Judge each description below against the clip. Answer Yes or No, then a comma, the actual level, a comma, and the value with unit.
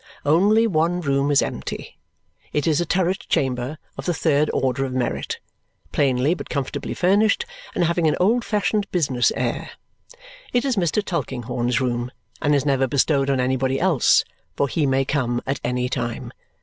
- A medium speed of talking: Yes, average, 165 wpm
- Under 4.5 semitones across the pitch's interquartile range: No, average, 5.2 semitones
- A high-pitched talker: No, medium, 140 Hz